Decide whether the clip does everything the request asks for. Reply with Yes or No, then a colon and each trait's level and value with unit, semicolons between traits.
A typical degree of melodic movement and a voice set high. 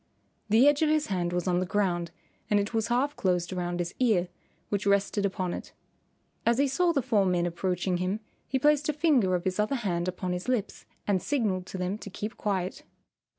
Yes: average, 4.9 semitones; high, 200 Hz